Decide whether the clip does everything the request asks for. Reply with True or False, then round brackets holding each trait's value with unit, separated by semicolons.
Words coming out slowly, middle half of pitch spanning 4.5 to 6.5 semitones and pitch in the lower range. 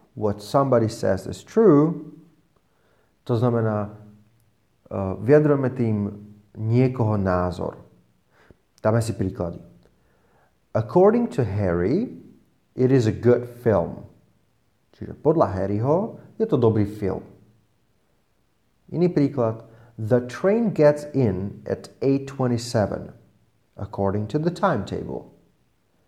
True (95 wpm; 5.0 semitones; 115 Hz)